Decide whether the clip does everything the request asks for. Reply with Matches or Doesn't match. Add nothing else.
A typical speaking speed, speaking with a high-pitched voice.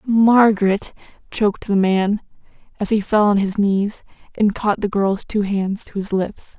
Matches